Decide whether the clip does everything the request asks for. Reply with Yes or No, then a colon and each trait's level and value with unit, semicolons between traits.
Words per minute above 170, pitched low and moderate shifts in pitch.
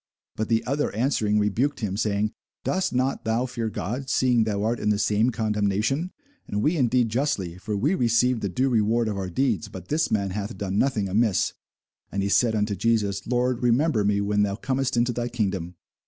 Yes: average, 200 wpm; low, 110 Hz; average, 3.5 semitones